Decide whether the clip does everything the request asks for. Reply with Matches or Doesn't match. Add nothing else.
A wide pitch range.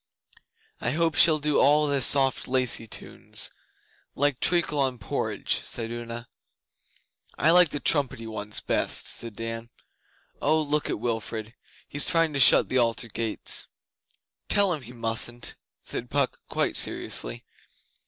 Doesn't match